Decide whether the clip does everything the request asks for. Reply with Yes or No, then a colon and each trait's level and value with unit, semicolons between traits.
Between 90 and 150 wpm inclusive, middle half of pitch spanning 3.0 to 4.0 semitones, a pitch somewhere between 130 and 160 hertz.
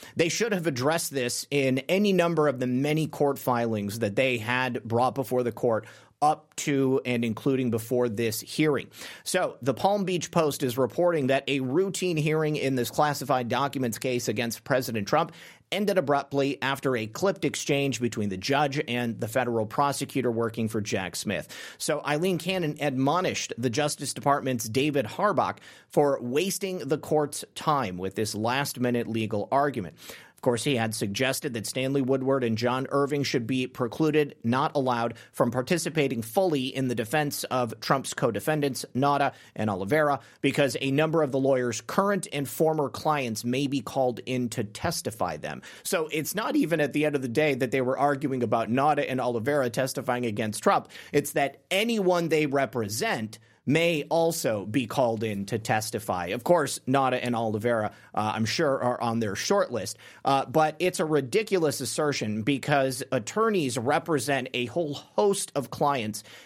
No: average, 170 wpm; average, 3.7 semitones; low, 135 Hz